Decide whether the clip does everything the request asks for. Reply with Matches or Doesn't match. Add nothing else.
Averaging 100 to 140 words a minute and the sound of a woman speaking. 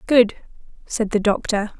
Matches